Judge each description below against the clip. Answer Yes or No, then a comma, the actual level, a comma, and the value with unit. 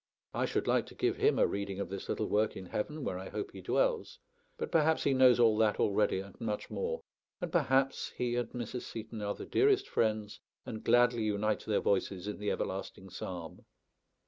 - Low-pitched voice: Yes, low, 110 Hz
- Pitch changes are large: No, average, 4.6 semitones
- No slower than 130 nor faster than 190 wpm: No, average, 200 wpm